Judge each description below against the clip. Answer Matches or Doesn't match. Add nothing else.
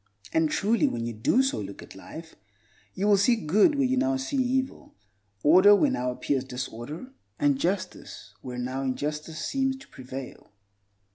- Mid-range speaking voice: Matches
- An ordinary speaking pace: Matches